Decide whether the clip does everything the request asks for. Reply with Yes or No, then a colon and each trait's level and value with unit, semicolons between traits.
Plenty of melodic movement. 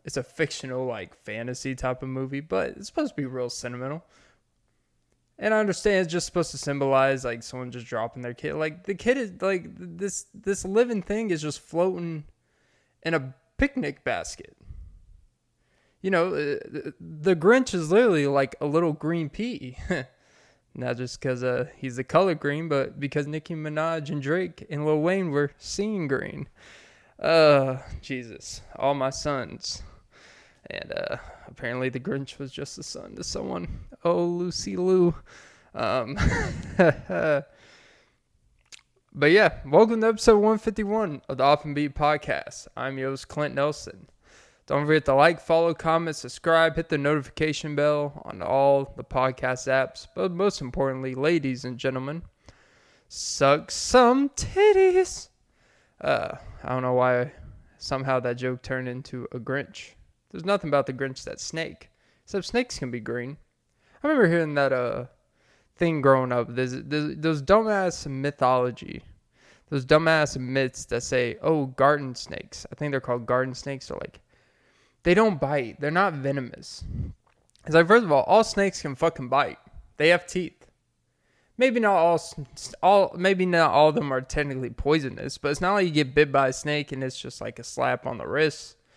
No: average, 4.8 semitones